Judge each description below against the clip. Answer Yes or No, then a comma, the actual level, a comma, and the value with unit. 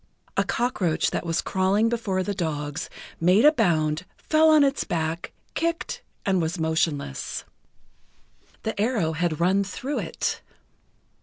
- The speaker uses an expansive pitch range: Yes, wide, 6.1 semitones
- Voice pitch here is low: No, medium, 185 Hz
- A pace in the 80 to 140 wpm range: Yes, slow, 135 wpm